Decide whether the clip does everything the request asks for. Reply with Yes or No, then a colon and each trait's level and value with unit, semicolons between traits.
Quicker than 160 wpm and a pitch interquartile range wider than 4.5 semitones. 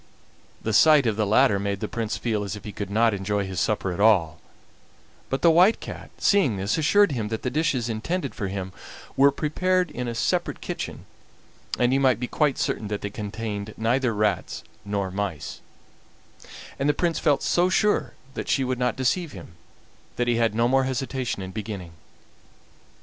Yes: average, 190 wpm; average, 5.0 semitones